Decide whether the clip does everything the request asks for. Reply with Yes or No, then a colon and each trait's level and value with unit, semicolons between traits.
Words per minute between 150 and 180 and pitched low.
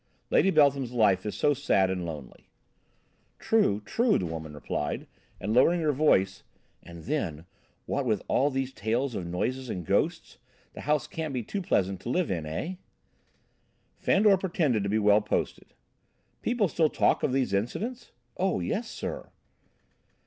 Yes: average, 155 wpm; low, 125 Hz